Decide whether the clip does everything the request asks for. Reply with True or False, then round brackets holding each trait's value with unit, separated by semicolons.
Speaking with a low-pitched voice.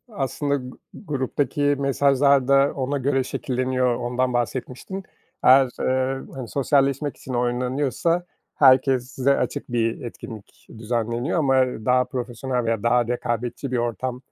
True (130 Hz)